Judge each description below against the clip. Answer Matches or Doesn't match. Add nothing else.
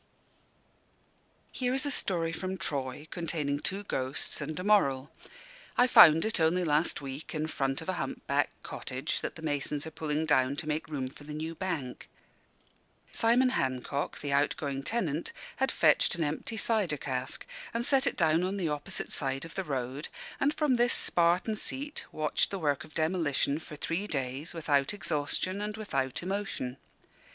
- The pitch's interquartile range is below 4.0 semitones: Doesn't match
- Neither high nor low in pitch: Matches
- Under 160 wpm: Doesn't match